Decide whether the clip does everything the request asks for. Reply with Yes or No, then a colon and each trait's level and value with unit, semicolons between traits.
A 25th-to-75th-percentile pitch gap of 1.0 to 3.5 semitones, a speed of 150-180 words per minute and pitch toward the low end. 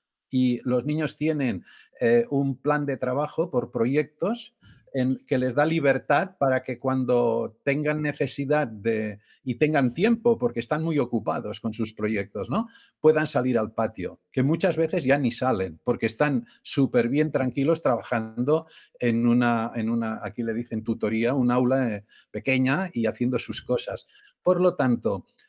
No: average, 4.3 semitones; average, 160 wpm; low, 130 Hz